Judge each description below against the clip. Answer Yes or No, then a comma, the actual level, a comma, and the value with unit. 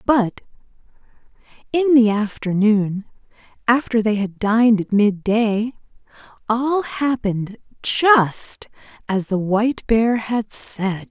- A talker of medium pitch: No, high, 220 Hz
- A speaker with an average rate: No, slow, 105 wpm